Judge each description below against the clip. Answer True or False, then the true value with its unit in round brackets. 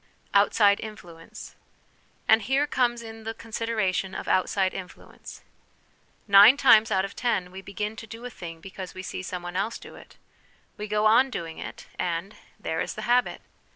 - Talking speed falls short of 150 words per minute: False (175 wpm)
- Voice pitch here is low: False (210 Hz)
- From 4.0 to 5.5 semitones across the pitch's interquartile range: False (3.3 semitones)